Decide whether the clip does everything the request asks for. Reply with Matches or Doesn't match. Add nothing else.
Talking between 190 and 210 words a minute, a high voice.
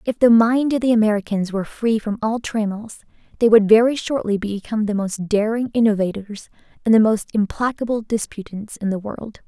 Doesn't match